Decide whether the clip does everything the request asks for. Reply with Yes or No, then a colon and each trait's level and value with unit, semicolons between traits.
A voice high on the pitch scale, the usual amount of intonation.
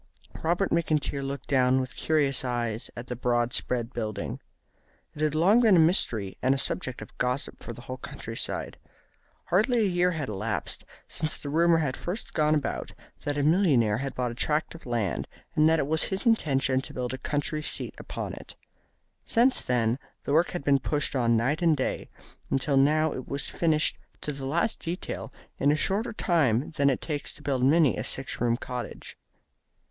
No: medium, 140 Hz; average, 4.2 semitones